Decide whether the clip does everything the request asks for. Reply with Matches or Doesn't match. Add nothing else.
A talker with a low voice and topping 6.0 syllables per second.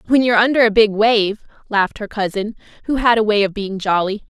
Doesn't match